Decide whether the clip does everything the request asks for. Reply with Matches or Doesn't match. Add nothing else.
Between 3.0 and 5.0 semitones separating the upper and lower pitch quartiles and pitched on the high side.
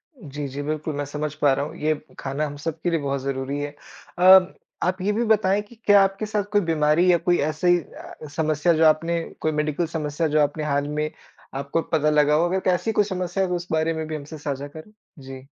Doesn't match